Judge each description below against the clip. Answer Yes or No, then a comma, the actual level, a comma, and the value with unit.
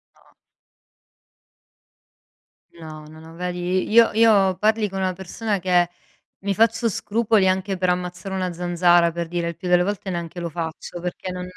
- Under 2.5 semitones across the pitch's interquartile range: Yes, narrow, 2.0 semitones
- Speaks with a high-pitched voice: No, medium, 180 Hz